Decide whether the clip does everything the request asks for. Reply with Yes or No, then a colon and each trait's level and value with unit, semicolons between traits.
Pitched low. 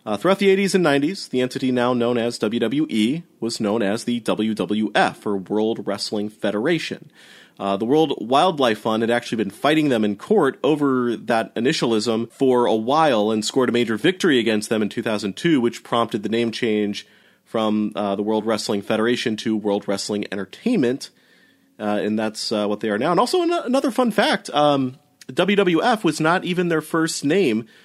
Yes: low, 115 Hz